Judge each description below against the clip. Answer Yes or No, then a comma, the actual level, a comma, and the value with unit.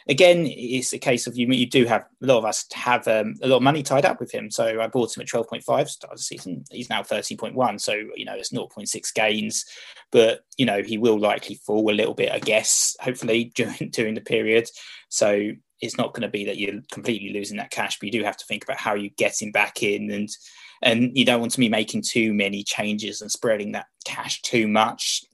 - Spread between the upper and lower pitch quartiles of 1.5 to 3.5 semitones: Yes, average, 2.8 semitones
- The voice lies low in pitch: Yes, low, 110 Hz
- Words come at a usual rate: No, fast, 245 wpm